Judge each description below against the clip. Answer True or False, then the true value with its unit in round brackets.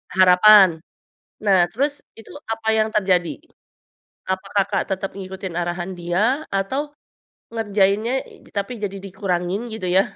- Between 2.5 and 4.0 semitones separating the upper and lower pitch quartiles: True (2.9 semitones)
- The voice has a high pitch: True (195 Hz)